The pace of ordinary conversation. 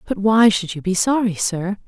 No: fast, 225 wpm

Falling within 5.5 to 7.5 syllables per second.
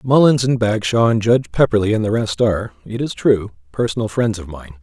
Yes: 5.8 syllables/s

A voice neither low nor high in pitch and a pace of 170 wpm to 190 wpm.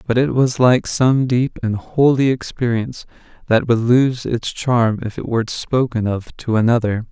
No: low, 120 Hz; average, 175 wpm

